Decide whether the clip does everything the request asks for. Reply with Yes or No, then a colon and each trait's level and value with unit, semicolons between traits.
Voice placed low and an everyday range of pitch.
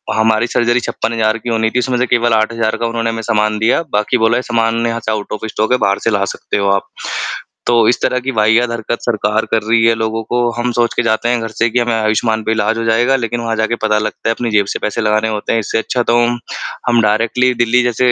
No: low, 115 Hz; narrow, 1.5 semitones